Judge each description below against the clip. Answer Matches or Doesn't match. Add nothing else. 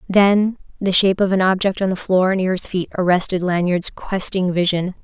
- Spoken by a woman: Matches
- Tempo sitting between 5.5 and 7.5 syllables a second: Doesn't match